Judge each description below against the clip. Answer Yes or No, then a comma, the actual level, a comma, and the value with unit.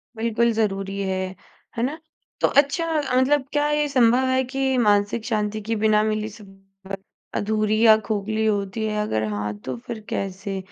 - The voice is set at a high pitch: Yes, high, 215 Hz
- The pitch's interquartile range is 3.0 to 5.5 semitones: Yes, average, 3.8 semitones